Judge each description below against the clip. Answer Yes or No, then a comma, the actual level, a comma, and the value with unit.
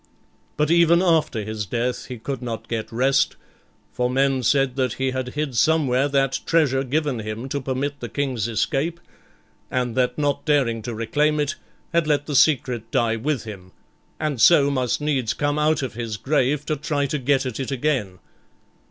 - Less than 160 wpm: No, average, 180 wpm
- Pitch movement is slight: No, average, 3.5 semitones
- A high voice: No, low, 135 Hz